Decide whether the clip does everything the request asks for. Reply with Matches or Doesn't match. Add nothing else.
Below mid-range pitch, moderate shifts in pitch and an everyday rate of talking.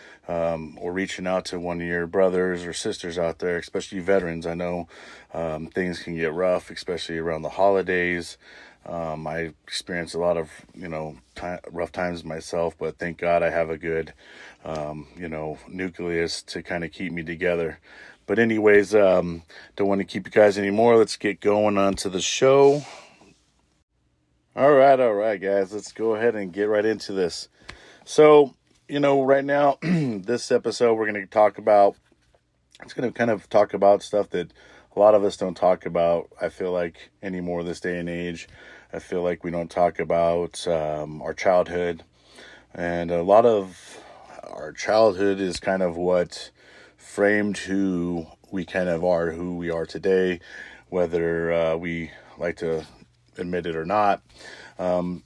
Matches